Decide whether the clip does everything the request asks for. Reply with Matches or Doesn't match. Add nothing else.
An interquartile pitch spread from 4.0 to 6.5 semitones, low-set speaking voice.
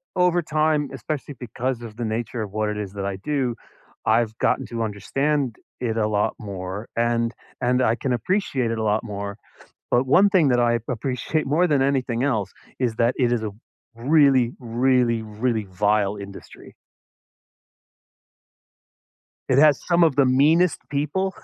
Matches